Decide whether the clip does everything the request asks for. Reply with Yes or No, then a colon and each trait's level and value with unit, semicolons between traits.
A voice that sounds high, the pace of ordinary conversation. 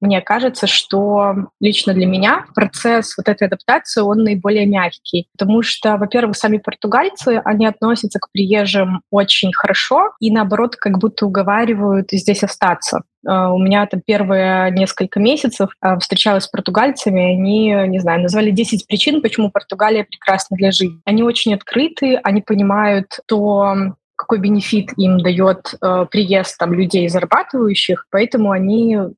Yes: high, 205 Hz; average, 140 wpm